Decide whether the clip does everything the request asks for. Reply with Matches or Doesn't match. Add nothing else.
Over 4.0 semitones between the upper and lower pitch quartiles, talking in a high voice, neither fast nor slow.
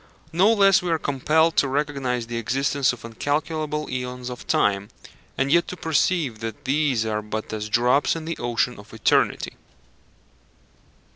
Doesn't match